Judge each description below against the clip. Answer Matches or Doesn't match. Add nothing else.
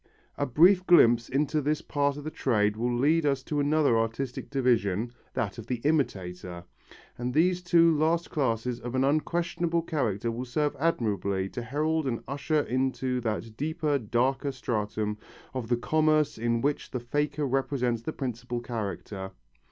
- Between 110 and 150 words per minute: Doesn't match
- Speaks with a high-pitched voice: Doesn't match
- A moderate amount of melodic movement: Matches